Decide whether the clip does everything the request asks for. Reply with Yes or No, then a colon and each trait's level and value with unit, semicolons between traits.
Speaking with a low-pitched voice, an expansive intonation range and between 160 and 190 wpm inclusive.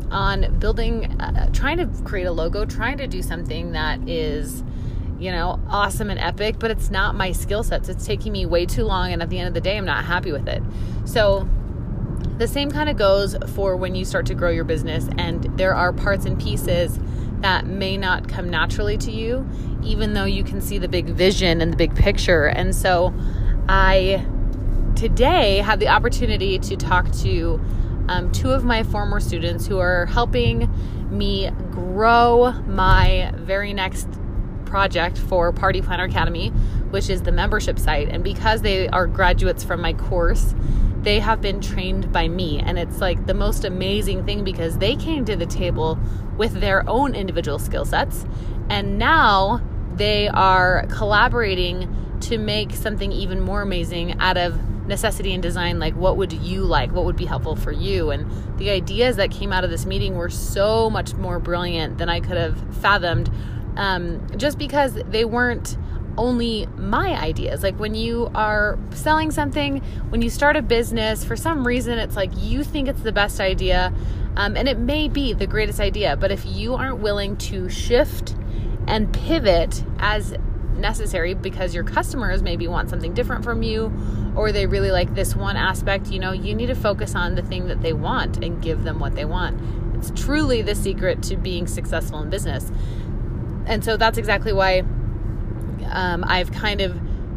No: low, 105 Hz; average, 3.3 semitones; average, 180 wpm